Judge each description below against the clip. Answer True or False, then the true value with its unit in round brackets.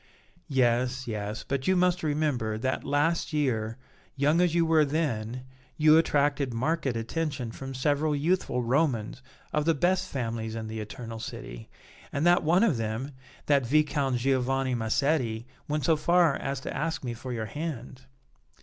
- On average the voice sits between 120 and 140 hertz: True (135 Hz)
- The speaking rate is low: False (160 wpm)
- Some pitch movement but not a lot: True (4.7 semitones)